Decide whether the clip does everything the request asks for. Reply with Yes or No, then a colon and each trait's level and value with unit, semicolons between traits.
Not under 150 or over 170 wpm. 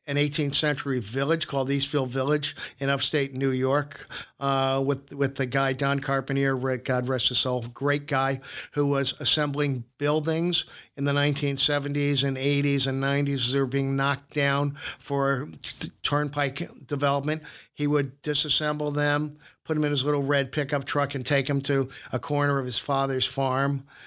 Yes: average, 160 wpm